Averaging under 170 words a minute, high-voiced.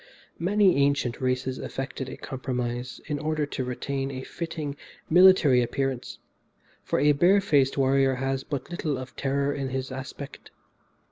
No: average, 145 wpm; low, 135 Hz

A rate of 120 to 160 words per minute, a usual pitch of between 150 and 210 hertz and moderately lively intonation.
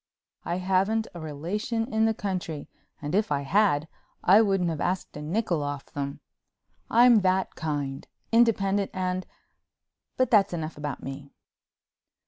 No: slow, 135 wpm; medium, 185 Hz; wide, 5.9 semitones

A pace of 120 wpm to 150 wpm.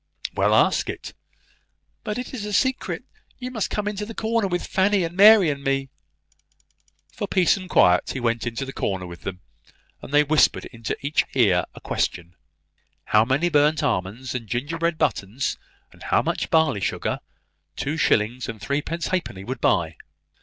No: average, 170 wpm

